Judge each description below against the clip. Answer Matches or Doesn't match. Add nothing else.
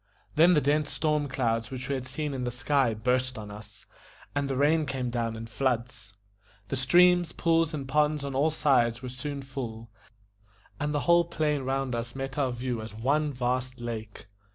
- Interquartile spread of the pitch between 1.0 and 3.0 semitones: Doesn't match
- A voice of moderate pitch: Doesn't match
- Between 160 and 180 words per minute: Doesn't match